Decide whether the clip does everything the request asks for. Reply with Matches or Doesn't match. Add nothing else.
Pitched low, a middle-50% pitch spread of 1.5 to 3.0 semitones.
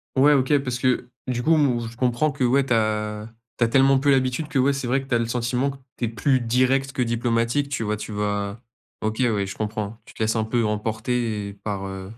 Doesn't match